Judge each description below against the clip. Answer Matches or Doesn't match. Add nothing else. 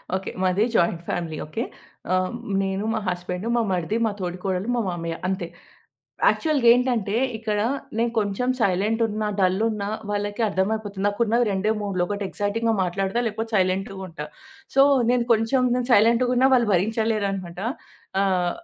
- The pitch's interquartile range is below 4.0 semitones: Matches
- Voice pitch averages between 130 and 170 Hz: Doesn't match